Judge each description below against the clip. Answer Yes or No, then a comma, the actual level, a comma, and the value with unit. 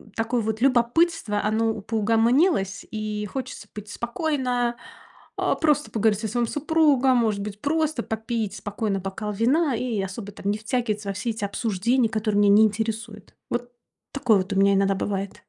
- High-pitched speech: Yes, high, 225 Hz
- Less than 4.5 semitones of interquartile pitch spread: Yes, average, 3.1 semitones